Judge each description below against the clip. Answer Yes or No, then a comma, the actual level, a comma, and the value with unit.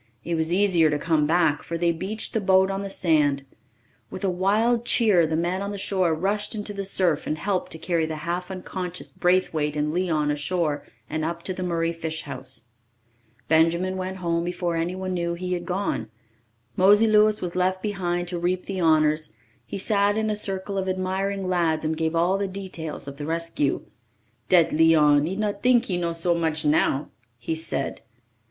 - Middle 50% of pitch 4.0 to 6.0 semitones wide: No, average, 3.0 semitones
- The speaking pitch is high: No, medium, 175 Hz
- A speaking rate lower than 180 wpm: No, average, 190 wpm